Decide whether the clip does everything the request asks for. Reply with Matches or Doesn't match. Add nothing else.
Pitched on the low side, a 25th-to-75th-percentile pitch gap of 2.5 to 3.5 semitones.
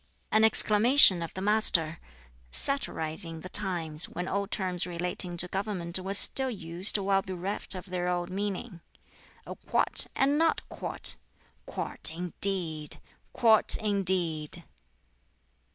Doesn't match